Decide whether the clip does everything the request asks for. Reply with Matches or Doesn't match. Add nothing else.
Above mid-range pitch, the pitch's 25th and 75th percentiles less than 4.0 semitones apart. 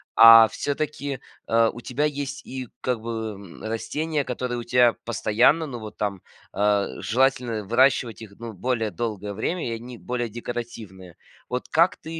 Doesn't match